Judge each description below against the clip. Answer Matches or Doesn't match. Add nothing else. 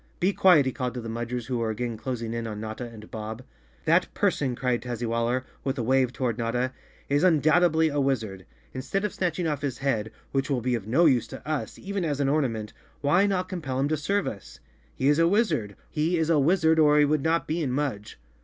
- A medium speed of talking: Doesn't match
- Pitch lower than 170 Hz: Matches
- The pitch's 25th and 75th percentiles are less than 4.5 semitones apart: Doesn't match